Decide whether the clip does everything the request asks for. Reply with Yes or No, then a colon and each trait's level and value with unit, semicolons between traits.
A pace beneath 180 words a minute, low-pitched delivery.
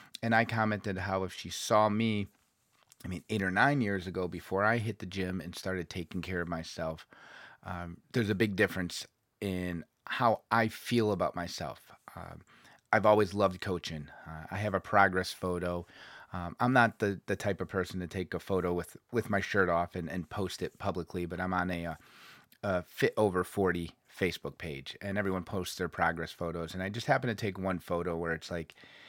No: average, 200 wpm; very low, 95 Hz